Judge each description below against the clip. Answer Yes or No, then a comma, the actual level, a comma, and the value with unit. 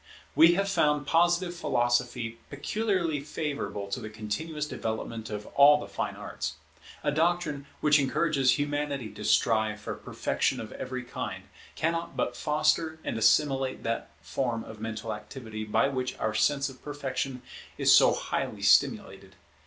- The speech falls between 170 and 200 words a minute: No, average, 145 wpm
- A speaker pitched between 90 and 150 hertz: Yes, medium, 140 Hz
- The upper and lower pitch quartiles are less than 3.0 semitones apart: No, average, 5.1 semitones